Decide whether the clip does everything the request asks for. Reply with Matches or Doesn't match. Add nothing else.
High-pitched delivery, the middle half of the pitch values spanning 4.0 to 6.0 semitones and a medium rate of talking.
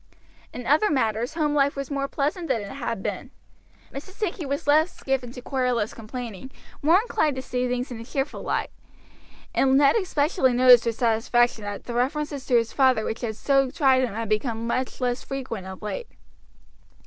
Doesn't match